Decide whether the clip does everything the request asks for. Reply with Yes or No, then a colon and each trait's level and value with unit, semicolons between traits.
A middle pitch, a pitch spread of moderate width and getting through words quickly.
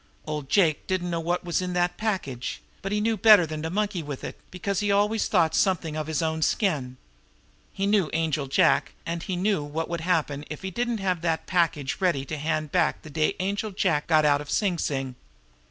Yes: medium, 170 Hz; average, 3.9 semitones; fast, 215 wpm